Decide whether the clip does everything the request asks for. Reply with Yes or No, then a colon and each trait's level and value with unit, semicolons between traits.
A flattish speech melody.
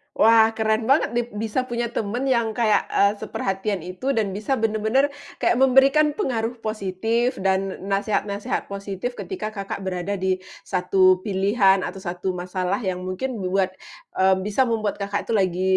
No: average, 3.5 semitones